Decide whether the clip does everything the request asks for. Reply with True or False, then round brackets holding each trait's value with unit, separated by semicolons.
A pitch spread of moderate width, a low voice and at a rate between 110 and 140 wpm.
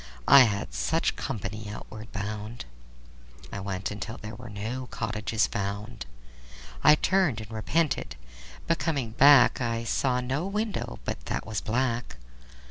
True (3.7 semitones; 115 Hz; 135 wpm)